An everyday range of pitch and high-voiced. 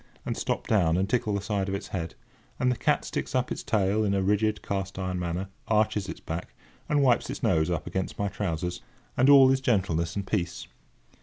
No: average, 3.3 semitones; low, 100 Hz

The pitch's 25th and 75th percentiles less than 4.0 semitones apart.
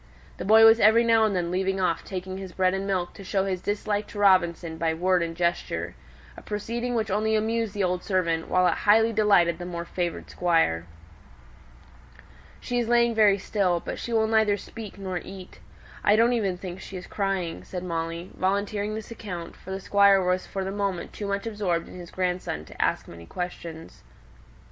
Yes: average, 2.9 semitones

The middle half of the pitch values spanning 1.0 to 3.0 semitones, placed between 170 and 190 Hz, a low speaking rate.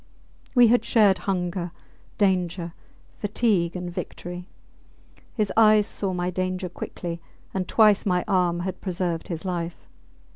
Yes: narrow, 2.4 semitones; medium, 185 Hz; slow, 125 wpm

